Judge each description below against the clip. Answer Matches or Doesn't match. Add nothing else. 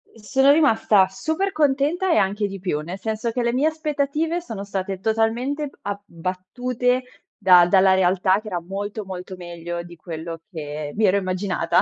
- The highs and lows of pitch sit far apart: Matches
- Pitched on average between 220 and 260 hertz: Doesn't match